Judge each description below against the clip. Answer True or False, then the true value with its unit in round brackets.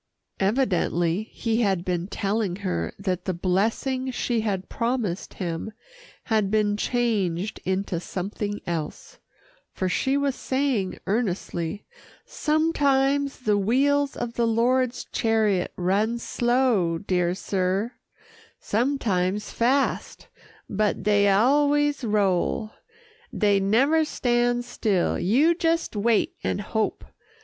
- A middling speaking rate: False (110 wpm)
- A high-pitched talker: True (215 Hz)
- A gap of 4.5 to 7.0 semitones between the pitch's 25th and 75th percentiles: True (4.8 semitones)